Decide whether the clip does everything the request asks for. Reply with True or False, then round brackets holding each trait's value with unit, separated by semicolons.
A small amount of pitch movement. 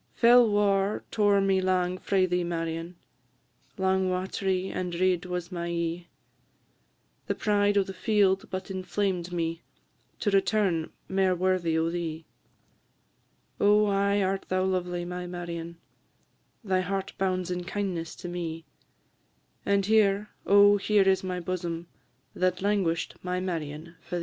True (2.1 semitones)